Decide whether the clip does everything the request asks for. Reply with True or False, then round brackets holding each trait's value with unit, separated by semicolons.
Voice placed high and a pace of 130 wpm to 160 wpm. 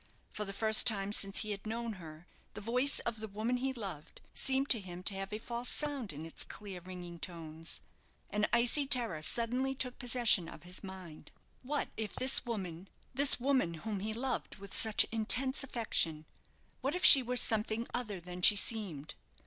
False (215 Hz; 185 wpm)